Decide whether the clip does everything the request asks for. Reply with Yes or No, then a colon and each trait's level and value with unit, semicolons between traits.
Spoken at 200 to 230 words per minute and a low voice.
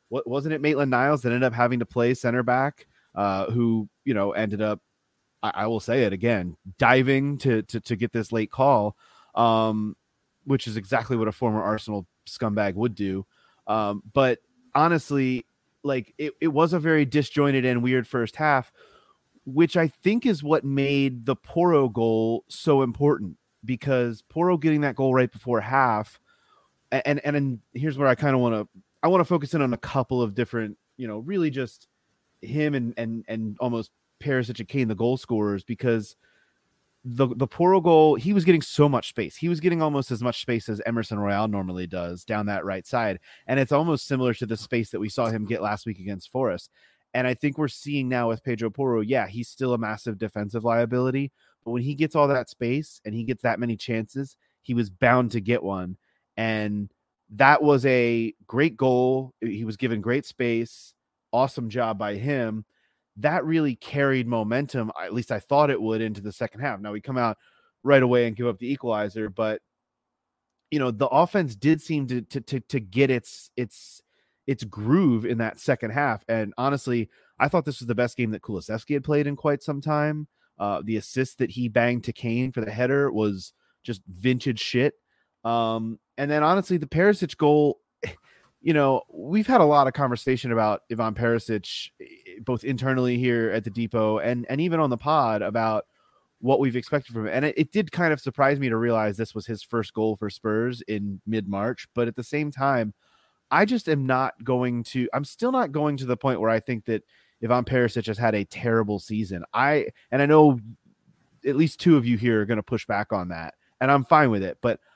Yes: fast, 205 wpm; low, 125 Hz